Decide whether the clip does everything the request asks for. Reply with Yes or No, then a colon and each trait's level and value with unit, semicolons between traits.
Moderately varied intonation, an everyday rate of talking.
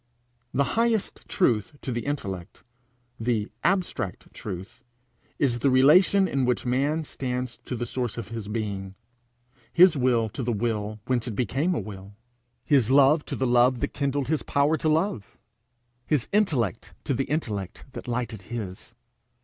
Yes: average, 4.7 semitones; average, 155 wpm